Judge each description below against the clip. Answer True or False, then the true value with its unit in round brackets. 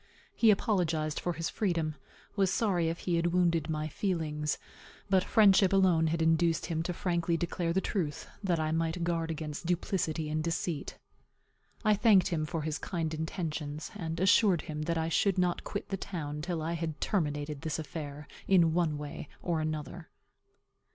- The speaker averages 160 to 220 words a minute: True (170 wpm)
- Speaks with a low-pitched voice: False (165 Hz)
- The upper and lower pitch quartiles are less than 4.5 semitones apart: True (2.4 semitones)